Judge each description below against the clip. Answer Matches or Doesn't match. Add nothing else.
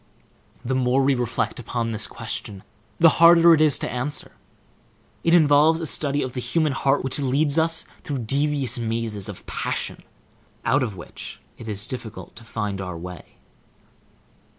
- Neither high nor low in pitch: Doesn't match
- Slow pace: Doesn't match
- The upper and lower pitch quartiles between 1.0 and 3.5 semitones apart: Doesn't match